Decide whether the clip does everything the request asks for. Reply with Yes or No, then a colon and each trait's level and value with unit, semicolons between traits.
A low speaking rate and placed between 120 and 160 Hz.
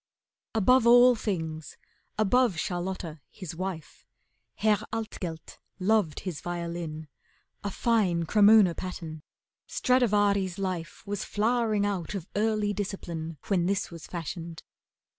No: slow, 110 wpm; high, 190 Hz